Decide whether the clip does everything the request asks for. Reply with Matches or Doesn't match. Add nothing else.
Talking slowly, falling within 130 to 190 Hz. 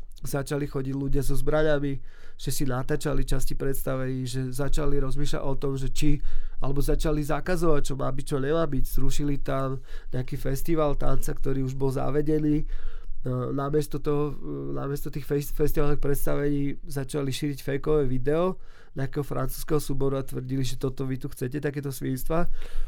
Doesn't match